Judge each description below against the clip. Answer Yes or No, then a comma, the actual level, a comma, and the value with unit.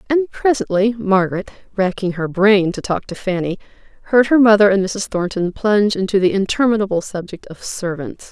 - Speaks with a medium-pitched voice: No, high, 200 Hz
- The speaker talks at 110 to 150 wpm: No, average, 165 wpm